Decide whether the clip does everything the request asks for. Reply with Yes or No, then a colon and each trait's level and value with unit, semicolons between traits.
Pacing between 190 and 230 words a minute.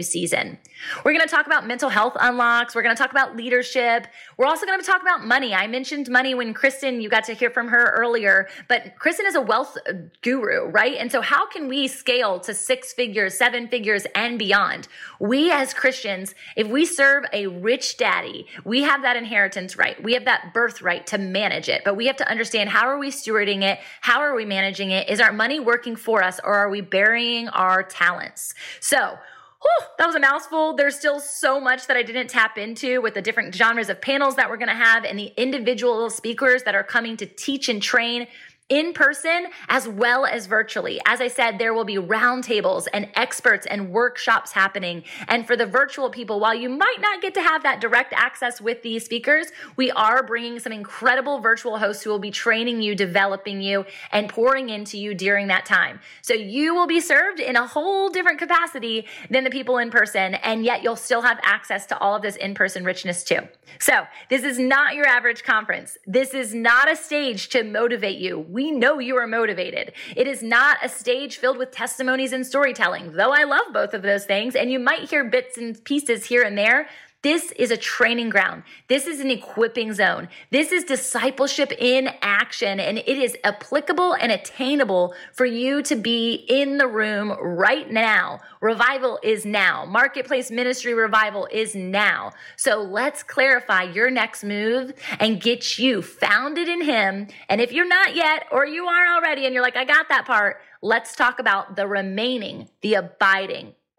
Yes: average, 200 wpm